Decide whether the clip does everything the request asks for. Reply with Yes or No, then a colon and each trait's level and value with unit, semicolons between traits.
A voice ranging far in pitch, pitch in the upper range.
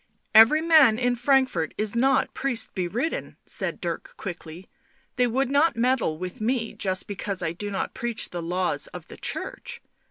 Yes: wide, 6.0 semitones; high, 230 Hz